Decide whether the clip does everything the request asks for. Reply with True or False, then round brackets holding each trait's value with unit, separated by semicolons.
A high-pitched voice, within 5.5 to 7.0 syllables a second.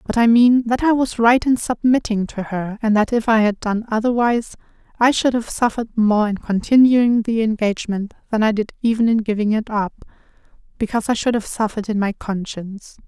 True (225 Hz; 5.6 syllables/s)